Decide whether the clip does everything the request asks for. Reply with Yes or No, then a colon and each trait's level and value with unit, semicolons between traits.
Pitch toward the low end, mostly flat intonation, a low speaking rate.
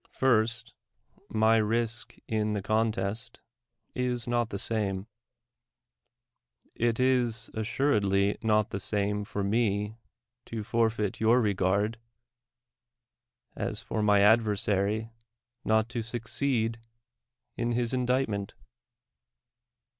Yes: low, 110 Hz; narrow, 2.3 semitones; slow, 95 wpm